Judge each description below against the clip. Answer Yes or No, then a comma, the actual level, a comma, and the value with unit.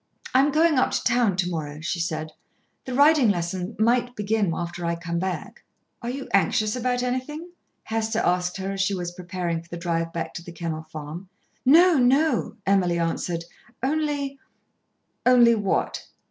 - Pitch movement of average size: No, wide, 6.5 semitones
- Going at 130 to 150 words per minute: No, average, 175 wpm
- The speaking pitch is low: No, high, 195 Hz